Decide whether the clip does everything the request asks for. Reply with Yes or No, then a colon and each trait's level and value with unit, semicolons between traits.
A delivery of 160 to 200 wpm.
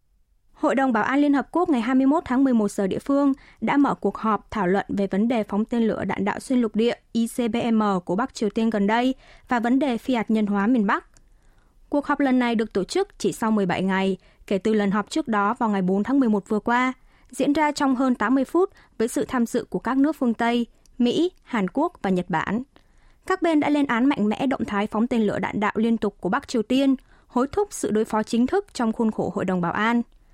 No: fast, 250 wpm